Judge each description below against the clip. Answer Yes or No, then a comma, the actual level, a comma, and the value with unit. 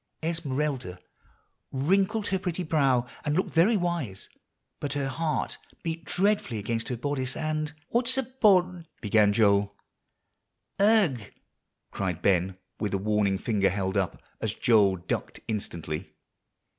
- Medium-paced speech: No, slow, 130 wpm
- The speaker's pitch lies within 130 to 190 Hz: Yes, low, 135 Hz